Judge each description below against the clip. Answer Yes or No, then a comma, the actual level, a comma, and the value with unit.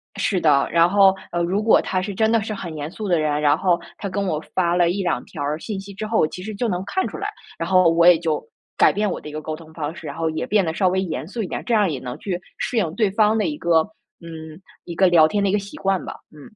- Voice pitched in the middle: Yes, medium, 180 Hz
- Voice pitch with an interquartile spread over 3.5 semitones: Yes, average, 4.1 semitones